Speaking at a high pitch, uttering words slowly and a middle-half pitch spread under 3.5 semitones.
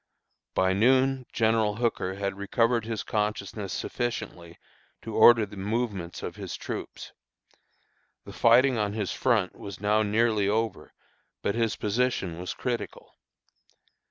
No: low, 110 Hz; slow, 130 wpm; average, 2.8 semitones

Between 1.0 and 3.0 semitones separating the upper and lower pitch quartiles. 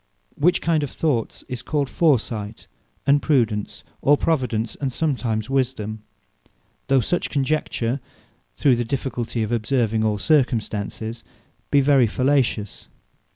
No: average, 4.2 semitones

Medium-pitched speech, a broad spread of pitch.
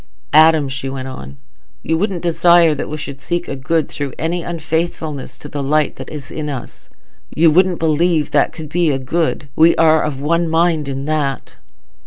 No: medium, 155 Hz; average, 2.9 semitones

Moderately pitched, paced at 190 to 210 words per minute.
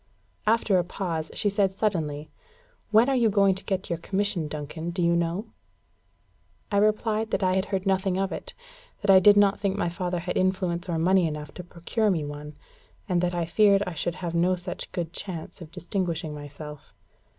Yes: medium, 180 Hz; average, 195 wpm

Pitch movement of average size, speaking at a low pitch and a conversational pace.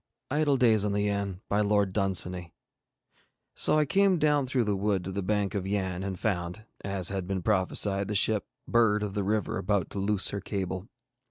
No: narrow, 2.3 semitones; low, 100 Hz; average, 180 wpm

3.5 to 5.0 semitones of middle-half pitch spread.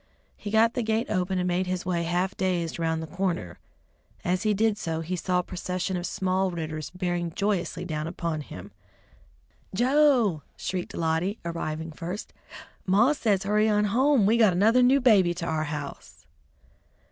Yes: average, 3.8 semitones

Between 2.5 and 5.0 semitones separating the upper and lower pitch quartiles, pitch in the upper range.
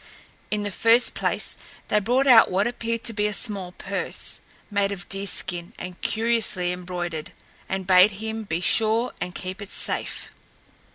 Yes: average, 3.5 semitones; high, 200 Hz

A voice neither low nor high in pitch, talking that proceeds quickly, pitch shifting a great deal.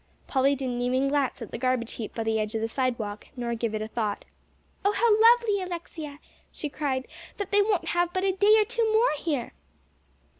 No: very high, 280 Hz; fast, 210 wpm; wide, 9.0 semitones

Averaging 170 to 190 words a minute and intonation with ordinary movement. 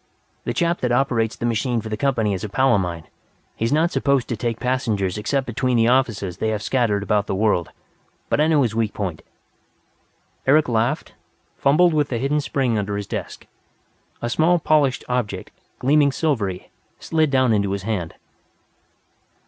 Yes: average, 180 wpm; average, 4.8 semitones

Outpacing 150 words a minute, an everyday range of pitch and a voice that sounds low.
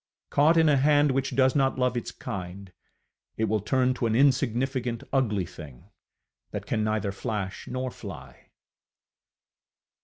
No: average, 145 wpm; average, 4.2 semitones; low, 125 Hz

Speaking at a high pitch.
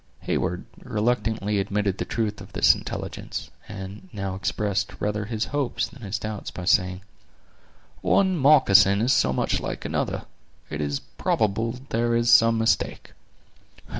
No: low, 105 Hz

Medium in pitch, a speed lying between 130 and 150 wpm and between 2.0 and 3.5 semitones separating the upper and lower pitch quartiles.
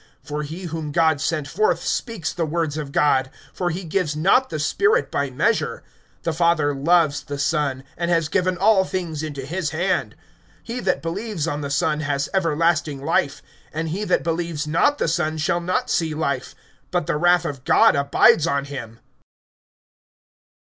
No: medium, 160 Hz; average, 175 wpm; average, 3.2 semitones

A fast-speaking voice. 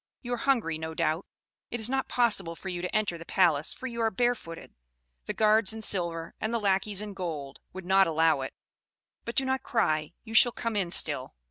Yes: fast, 215 wpm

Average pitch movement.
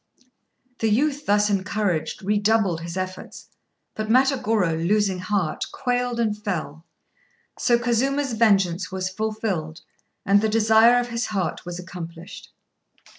Yes: average, 3.8 semitones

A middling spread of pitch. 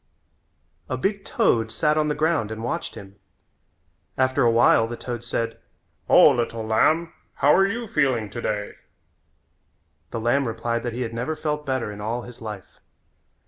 Yes: average, 4.7 semitones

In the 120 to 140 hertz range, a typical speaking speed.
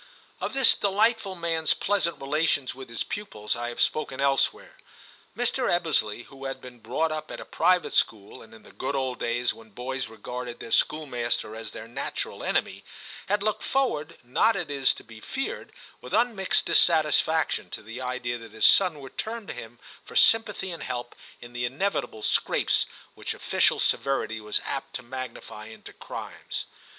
Yes: low, 135 Hz; average, 175 wpm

